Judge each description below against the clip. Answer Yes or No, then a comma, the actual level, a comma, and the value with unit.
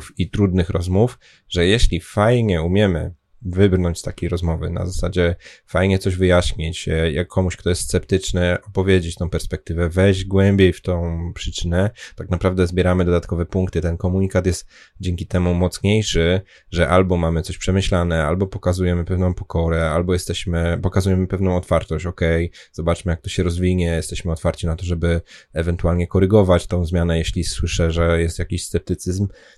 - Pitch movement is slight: Yes, narrow, 1.7 semitones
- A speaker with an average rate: Yes, average, 150 wpm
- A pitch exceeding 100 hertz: No, very low, 90 Hz